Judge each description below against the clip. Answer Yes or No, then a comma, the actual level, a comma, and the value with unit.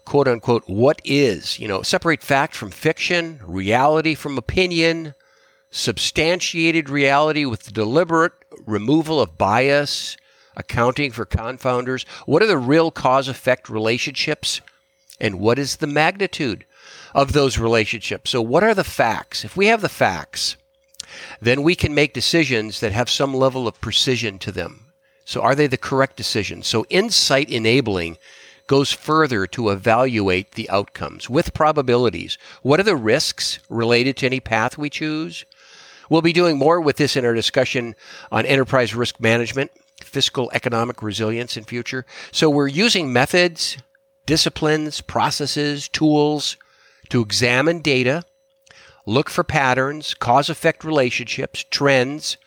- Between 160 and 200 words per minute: No, slow, 135 wpm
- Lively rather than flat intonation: No, average, 4.9 semitones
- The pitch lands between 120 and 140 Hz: Yes, low, 135 Hz